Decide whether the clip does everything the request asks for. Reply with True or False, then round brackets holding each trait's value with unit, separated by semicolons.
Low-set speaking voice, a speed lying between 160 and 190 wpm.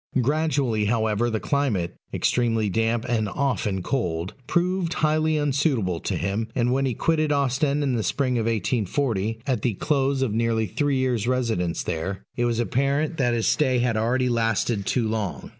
True (120 Hz; 170 wpm)